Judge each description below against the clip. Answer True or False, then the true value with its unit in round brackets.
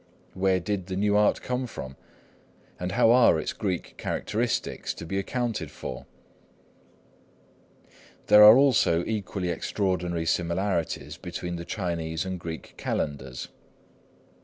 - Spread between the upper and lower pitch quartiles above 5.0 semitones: False (3.7 semitones)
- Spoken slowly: True (120 wpm)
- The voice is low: True (95 Hz)